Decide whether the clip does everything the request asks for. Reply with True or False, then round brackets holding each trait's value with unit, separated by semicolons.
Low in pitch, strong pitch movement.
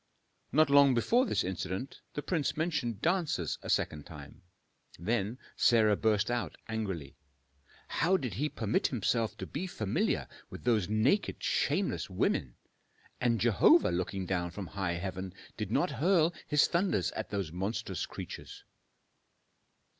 True (110 Hz; 7.0 semitones)